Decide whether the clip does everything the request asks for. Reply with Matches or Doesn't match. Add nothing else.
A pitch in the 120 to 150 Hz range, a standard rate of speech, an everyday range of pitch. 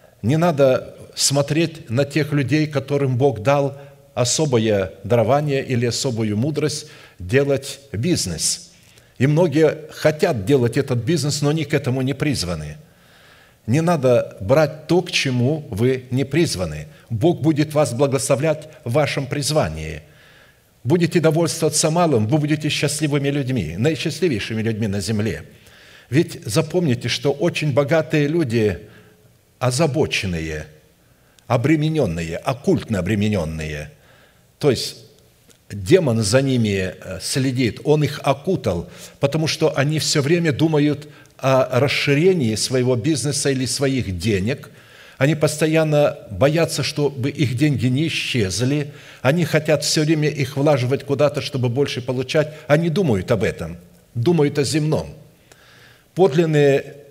Matches